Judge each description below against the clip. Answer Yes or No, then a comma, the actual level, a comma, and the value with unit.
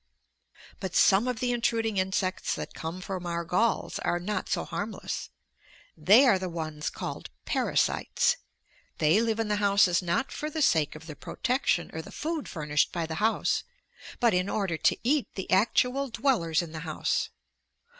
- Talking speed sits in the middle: Yes, average, 170 wpm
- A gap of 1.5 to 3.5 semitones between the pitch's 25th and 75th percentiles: No, wide, 5.4 semitones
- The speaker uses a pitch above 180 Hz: Yes, high, 190 Hz